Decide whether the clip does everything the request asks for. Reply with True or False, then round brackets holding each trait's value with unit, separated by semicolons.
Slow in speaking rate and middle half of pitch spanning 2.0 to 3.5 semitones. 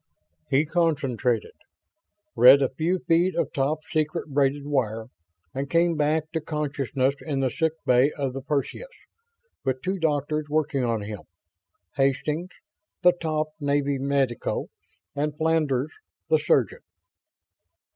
True (125 wpm; 2.8 semitones)